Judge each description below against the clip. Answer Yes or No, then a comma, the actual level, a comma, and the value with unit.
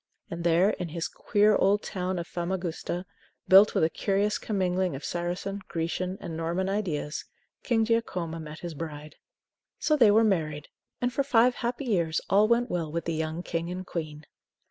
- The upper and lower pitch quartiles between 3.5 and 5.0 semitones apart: Yes, average, 4.0 semitones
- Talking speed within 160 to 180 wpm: Yes, average, 175 wpm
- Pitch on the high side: No, medium, 180 Hz